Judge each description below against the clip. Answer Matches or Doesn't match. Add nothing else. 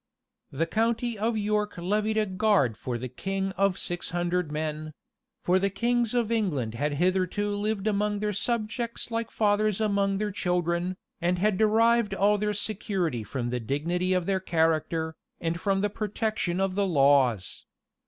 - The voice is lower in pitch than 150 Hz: Doesn't match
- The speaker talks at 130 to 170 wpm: Matches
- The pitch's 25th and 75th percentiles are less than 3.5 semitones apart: Doesn't match